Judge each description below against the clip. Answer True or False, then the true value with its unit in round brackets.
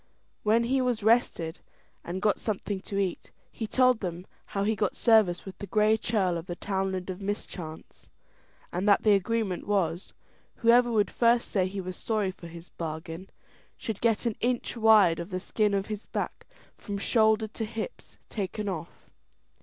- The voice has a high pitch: True (205 Hz)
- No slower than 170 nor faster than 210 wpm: True (175 wpm)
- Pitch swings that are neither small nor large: True (3.3 semitones)